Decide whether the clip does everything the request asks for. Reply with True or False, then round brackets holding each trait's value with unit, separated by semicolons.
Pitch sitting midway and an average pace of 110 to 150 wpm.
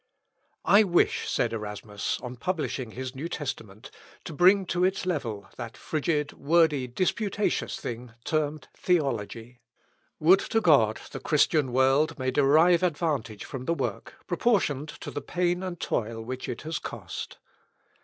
True (145 Hz; 145 wpm)